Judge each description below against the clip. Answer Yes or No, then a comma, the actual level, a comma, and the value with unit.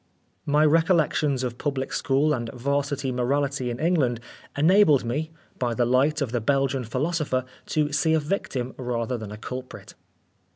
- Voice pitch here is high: No, low, 135 Hz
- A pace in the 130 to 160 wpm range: Yes, average, 155 wpm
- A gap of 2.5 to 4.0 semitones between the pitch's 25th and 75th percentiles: Yes, average, 3.4 semitones